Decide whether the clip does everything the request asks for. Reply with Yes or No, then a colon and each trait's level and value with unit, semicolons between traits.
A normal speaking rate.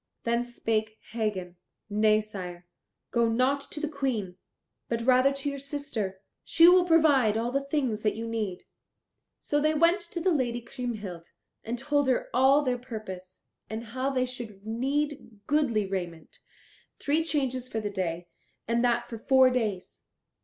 Yes: average, 155 wpm